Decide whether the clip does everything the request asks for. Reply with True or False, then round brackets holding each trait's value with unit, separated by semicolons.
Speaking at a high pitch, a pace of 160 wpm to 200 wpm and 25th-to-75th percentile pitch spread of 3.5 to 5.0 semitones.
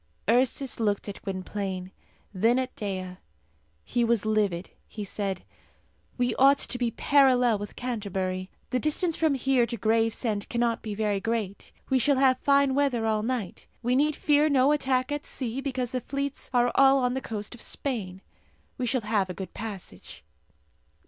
True (235 Hz; 170 wpm; 4.3 semitones)